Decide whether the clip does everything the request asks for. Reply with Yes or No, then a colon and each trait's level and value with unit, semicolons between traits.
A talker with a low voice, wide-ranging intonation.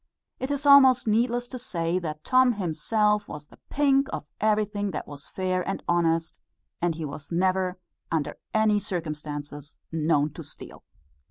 No: medium, 185 Hz; wide, 6.0 semitones